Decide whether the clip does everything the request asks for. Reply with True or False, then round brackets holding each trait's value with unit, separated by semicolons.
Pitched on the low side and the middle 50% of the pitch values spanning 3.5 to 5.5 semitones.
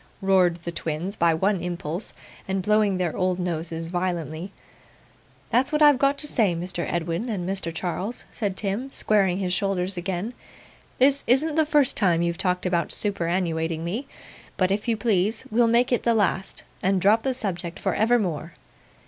False (190 Hz; 4.4 semitones)